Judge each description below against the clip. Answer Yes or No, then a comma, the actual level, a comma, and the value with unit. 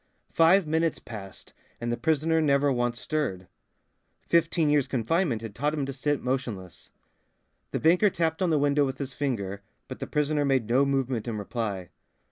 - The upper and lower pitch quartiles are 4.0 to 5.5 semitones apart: Yes, average, 4.7 semitones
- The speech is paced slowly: No, average, 170 wpm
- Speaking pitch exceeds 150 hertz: No, medium, 140 Hz